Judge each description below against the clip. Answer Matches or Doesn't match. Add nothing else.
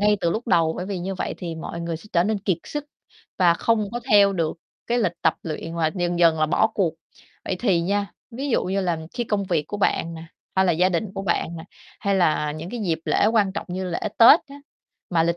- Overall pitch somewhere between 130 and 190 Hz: Matches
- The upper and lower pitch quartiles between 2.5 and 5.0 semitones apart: Matches